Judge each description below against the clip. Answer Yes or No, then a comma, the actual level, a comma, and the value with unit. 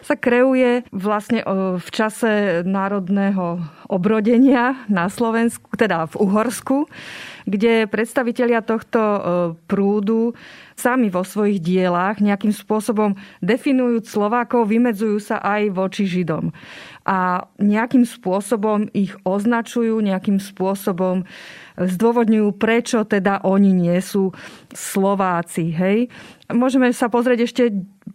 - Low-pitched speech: No, high, 210 Hz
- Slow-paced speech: Yes, slow, 100 wpm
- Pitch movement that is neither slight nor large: Yes, average, 3.3 semitones